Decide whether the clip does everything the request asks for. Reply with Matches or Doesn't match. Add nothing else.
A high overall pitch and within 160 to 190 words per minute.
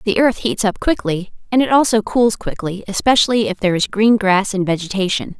Doesn't match